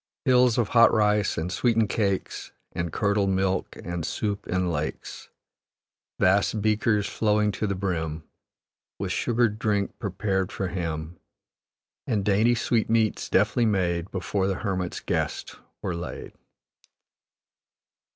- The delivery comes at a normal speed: No, slow, 120 wpm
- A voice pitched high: No, low, 100 Hz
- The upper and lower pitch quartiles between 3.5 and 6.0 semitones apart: No, average, 2.9 semitones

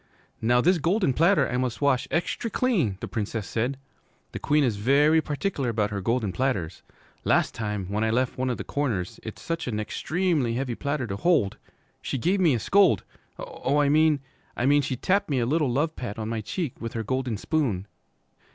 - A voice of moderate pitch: No, low, 130 Hz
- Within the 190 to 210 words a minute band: Yes, fast, 205 wpm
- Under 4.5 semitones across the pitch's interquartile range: No, wide, 5.5 semitones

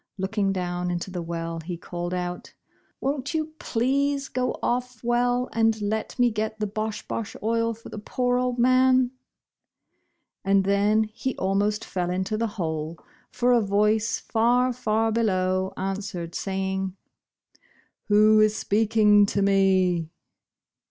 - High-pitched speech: Yes, high, 210 Hz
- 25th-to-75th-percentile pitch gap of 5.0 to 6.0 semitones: No, average, 3.8 semitones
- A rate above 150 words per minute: No, average, 140 wpm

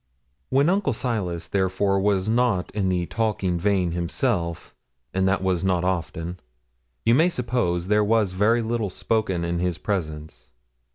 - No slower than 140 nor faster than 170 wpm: Yes, average, 150 wpm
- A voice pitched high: No, very low, 95 Hz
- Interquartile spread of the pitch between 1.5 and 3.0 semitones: No, average, 4.2 semitones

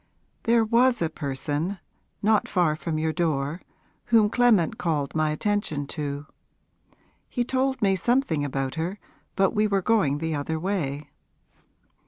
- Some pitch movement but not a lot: No, wide, 6.0 semitones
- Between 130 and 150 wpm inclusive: Yes, average, 140 wpm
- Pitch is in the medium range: Yes, medium, 170 Hz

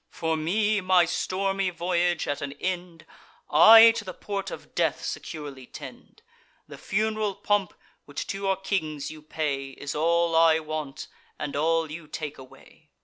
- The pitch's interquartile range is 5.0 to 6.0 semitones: No, average, 4.1 semitones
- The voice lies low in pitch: No, medium, 170 Hz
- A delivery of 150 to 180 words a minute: Yes, average, 155 wpm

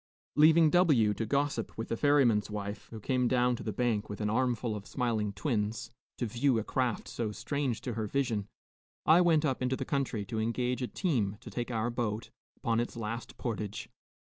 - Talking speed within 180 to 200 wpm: Yes, average, 195 wpm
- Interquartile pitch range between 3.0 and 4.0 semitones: Yes, average, 3.5 semitones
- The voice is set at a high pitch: No, low, 120 Hz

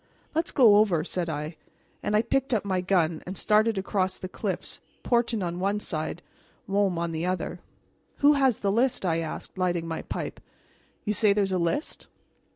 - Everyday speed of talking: Yes, average, 185 wpm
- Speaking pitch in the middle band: No, high, 195 Hz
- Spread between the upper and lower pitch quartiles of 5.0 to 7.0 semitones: No, average, 3.8 semitones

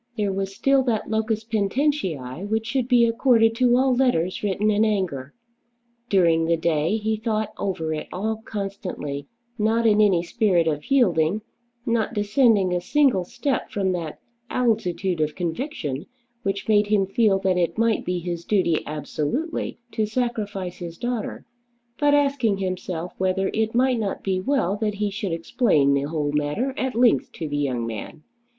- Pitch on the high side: Yes, high, 200 Hz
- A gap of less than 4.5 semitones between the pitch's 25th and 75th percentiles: No, average, 5.0 semitones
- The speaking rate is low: No, average, 165 wpm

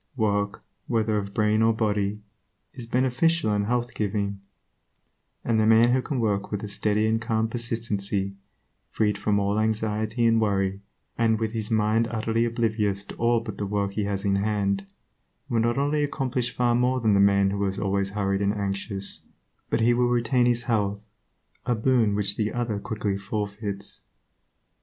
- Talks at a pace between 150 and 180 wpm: Yes, average, 175 wpm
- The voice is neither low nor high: No, low, 110 Hz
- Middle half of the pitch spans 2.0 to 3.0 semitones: Yes, narrow, 2.5 semitones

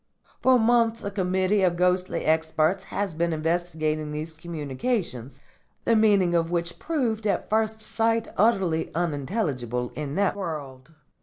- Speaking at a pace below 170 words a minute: Yes, slow, 135 wpm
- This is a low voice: No, medium, 175 Hz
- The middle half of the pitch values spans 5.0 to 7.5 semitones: Yes, average, 5.3 semitones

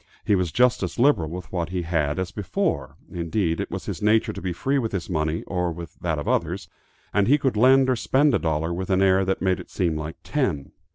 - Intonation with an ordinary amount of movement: Yes, average, 5.0 semitones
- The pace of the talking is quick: Yes, fast, 240 wpm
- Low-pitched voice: Yes, very low, 90 Hz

